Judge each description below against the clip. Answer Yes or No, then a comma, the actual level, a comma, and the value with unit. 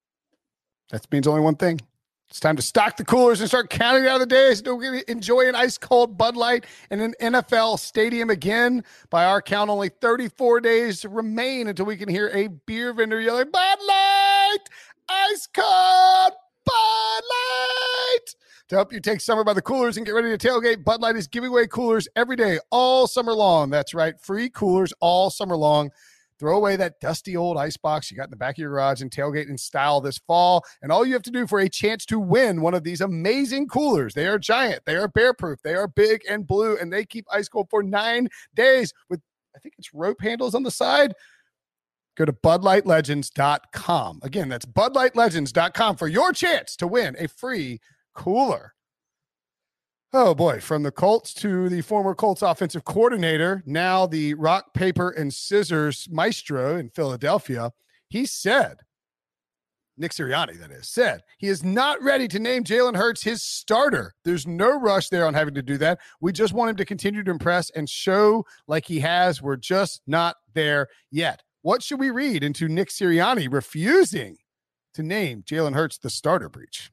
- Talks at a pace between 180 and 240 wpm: Yes, average, 185 wpm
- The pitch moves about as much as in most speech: No, wide, 7.0 semitones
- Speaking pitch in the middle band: No, high, 205 Hz